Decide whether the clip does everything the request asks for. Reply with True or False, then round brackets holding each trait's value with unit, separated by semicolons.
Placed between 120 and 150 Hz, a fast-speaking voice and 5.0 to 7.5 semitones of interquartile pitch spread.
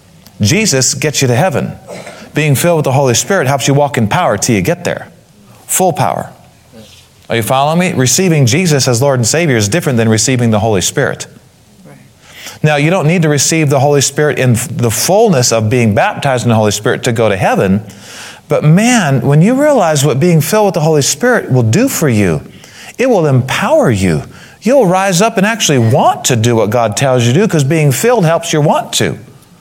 True (140 Hz; 210 wpm; 5.4 semitones)